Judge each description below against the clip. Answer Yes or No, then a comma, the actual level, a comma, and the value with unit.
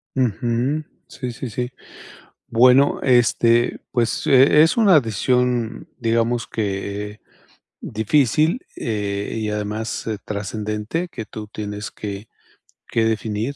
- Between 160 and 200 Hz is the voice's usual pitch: No, low, 115 Hz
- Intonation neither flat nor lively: Yes, average, 3.1 semitones